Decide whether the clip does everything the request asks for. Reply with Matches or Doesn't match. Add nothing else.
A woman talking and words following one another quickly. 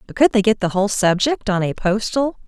Matches